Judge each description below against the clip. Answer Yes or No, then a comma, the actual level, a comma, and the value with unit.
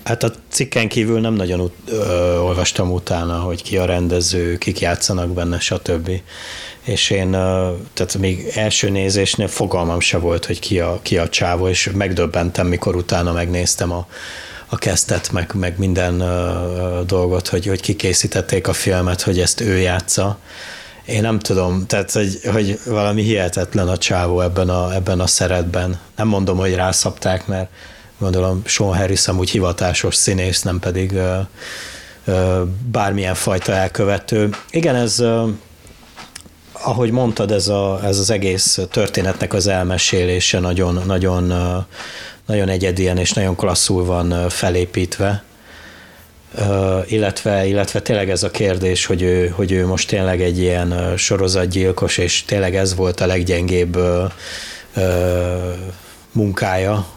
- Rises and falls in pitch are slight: Yes, narrow, 2.1 semitones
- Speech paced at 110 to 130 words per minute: No, average, 140 wpm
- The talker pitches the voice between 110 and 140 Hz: No, very low, 95 Hz